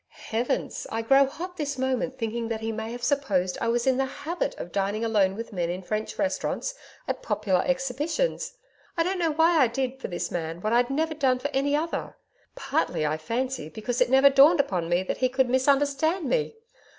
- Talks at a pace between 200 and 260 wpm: Yes, fast, 205 wpm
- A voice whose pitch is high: Yes, very high, 260 Hz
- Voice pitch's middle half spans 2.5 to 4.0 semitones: No, average, 4.6 semitones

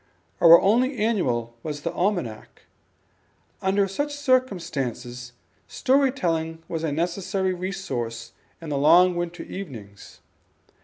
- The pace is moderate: No, slow, 110 wpm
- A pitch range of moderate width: No, wide, 6.2 semitones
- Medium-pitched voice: Yes, medium, 175 Hz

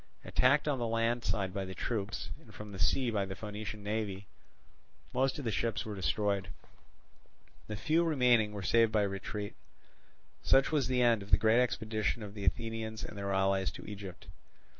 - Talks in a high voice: No, low, 110 Hz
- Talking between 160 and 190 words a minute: Yes, average, 185 wpm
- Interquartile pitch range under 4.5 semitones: Yes, average, 2.9 semitones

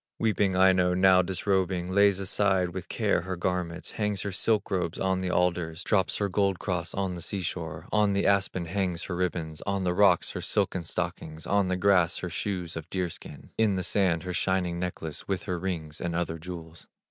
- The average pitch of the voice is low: Yes, very low, 90 Hz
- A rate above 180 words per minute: Yes, average, 200 wpm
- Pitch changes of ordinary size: No, narrow, 2.0 semitones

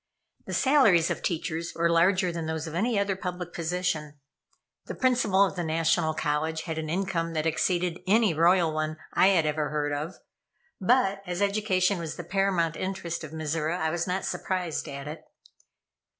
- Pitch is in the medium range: Yes, medium, 170 Hz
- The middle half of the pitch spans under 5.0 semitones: Yes, average, 3.0 semitones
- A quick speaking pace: No, average, 175 wpm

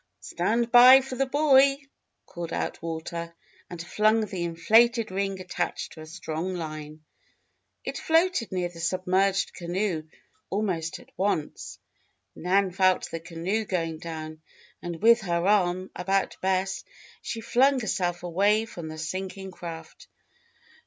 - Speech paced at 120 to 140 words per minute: Yes, slow, 135 wpm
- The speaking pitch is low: No, medium, 185 Hz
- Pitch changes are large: No, average, 4.3 semitones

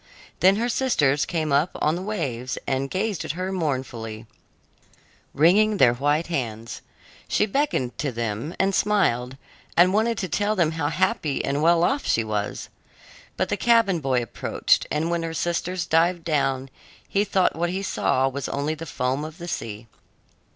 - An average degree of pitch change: No, wide, 5.8 semitones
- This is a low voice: No, medium, 160 Hz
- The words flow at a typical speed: Yes, average, 170 wpm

